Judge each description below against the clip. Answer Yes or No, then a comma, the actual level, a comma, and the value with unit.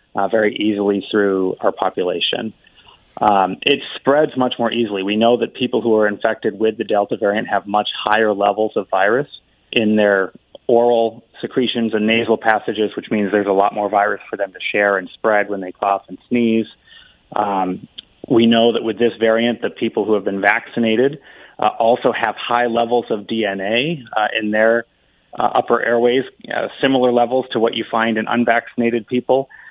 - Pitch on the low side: Yes, low, 110 Hz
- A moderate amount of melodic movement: No, narrow, 2.3 semitones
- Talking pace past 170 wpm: Yes, average, 180 wpm